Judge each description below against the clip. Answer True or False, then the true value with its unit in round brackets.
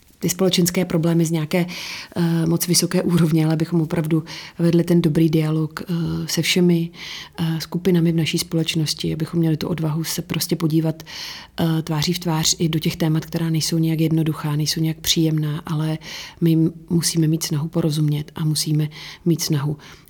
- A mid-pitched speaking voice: True (165 Hz)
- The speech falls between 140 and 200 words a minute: True (165 wpm)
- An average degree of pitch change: False (1.2 semitones)